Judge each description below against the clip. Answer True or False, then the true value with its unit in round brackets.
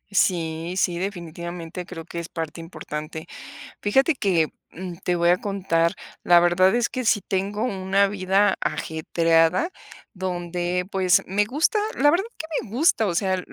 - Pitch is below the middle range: False (180 Hz)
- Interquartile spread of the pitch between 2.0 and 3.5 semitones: True (2.9 semitones)